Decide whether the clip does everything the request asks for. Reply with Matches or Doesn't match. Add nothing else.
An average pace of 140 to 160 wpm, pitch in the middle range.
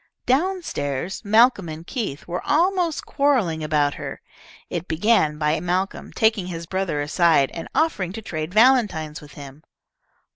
Matches